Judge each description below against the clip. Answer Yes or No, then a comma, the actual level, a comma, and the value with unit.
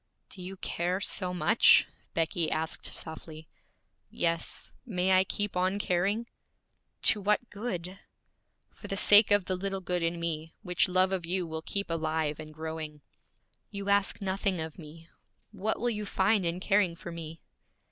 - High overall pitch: No, medium, 180 Hz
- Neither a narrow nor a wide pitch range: Yes, average, 3.3 semitones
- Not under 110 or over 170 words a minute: Yes, average, 160 wpm